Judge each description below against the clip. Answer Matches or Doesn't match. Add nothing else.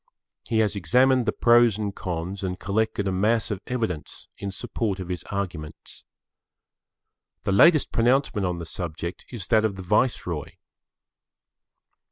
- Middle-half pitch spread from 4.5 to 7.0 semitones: Doesn't match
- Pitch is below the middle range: Matches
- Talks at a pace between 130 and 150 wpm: Matches